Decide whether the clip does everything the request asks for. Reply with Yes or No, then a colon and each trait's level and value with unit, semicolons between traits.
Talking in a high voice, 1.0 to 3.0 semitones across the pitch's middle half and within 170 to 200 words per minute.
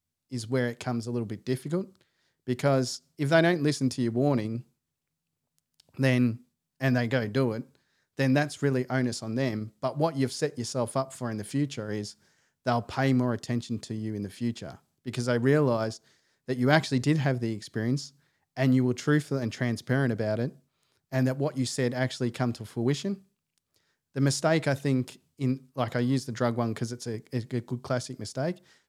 No: low, 130 Hz; narrow, 2.4 semitones; average, 195 wpm